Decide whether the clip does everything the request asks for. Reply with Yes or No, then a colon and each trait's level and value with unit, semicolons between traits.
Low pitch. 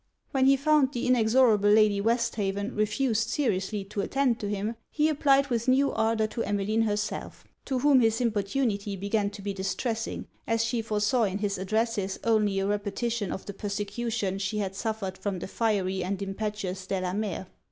No: high, 215 Hz